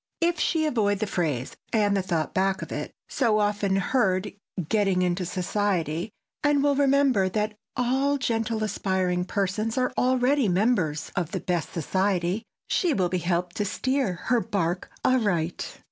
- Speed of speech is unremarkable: Yes, average, 145 wpm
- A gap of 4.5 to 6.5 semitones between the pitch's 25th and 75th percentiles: Yes, average, 5.3 semitones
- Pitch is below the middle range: No, high, 200 Hz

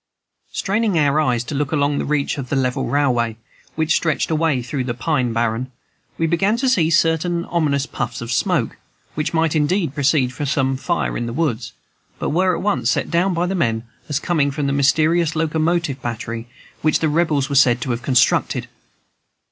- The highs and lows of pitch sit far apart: No, average, 4.3 semitones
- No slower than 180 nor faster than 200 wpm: Yes, average, 190 wpm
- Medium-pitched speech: Yes, medium, 145 Hz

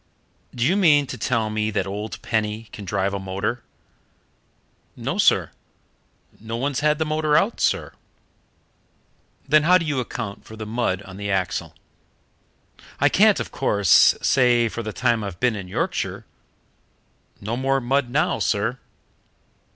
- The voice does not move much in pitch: No, average, 4.9 semitones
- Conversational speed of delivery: Yes, average, 150 wpm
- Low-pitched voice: Yes, low, 115 Hz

